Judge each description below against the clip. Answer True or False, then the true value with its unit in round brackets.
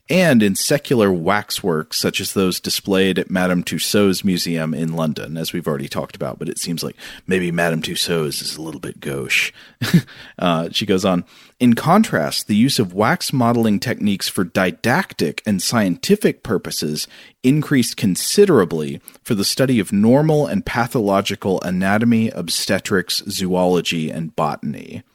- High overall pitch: False (100 Hz)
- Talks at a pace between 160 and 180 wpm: False (150 wpm)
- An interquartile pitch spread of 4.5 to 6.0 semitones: True (5.2 semitones)